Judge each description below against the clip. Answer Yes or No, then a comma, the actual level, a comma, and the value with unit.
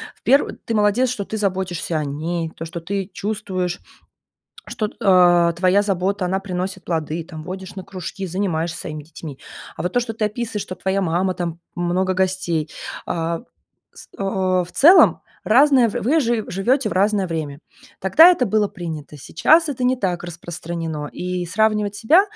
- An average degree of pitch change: Yes, average, 3.6 semitones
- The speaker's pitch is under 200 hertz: Yes, medium, 185 Hz